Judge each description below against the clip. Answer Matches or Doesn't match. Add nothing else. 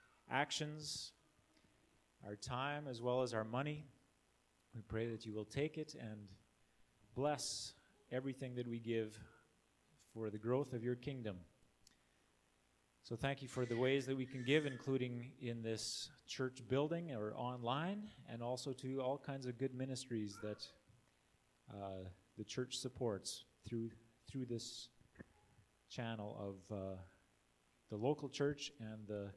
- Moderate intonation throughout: Matches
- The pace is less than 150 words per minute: Matches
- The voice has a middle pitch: Doesn't match